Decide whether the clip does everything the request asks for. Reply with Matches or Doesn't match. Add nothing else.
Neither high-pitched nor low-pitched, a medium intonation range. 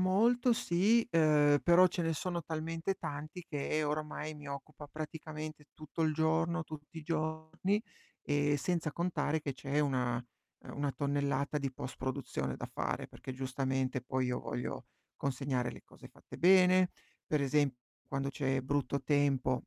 Matches